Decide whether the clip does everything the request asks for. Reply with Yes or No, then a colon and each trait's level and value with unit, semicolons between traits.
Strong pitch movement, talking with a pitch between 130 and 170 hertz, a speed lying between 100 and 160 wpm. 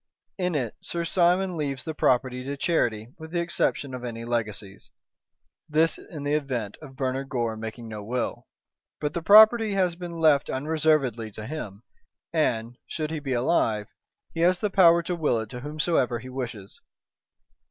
No: wide, 5.8 semitones; medium, 140 Hz; average, 170 wpm